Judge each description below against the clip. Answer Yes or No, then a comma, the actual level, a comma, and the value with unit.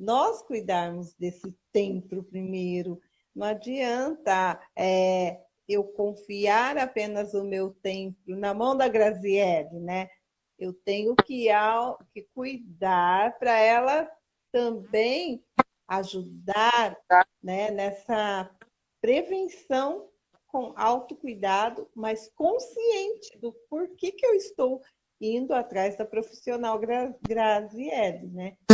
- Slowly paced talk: Yes, slow, 100 wpm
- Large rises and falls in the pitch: No, average, 4.6 semitones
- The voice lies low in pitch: No, high, 220 Hz